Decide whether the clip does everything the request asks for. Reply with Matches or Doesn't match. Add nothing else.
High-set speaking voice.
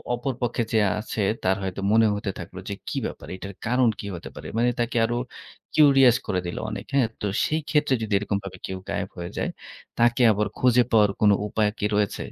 Doesn't match